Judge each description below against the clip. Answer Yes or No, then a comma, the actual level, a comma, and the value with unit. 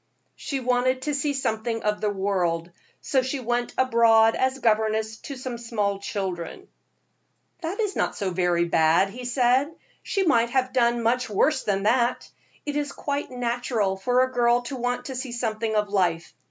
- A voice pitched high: Yes, high, 235 Hz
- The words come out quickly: No, average, 175 wpm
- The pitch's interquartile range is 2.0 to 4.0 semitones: Yes, average, 3.7 semitones